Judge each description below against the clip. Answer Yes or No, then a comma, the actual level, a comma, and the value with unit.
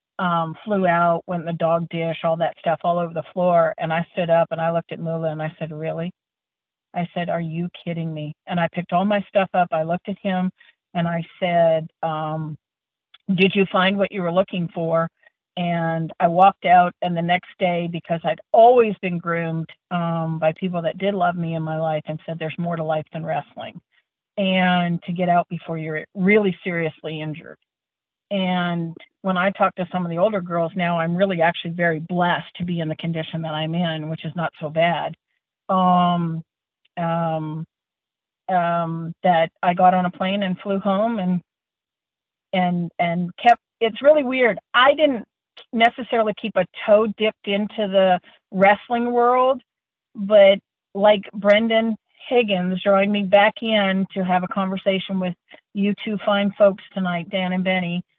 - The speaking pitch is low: No, medium, 175 Hz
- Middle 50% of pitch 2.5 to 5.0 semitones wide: Yes, average, 3.0 semitones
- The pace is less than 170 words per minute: No, average, 185 wpm